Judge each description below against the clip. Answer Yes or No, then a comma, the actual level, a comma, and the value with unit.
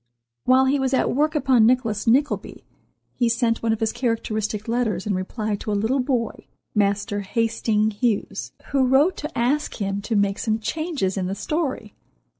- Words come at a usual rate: Yes, average, 165 wpm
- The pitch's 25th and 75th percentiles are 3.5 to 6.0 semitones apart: Yes, average, 3.9 semitones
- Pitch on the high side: Yes, high, 230 Hz